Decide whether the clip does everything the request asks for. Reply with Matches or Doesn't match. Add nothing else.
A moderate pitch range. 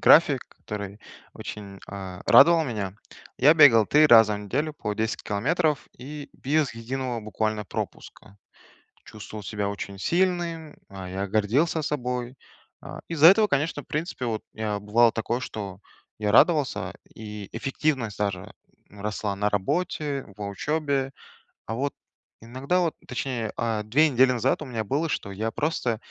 Doesn't match